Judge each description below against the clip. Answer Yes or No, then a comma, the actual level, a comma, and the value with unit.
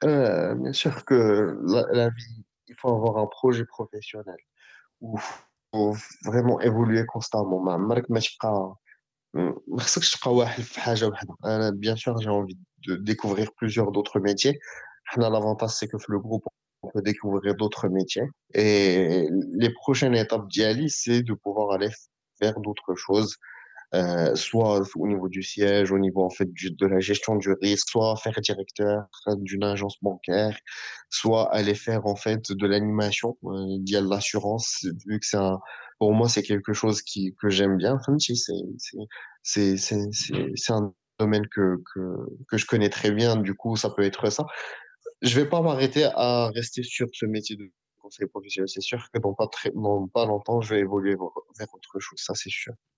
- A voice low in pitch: Yes, low, 105 Hz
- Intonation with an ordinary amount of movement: No, narrow, 2.3 semitones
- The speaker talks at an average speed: No, fast, 175 wpm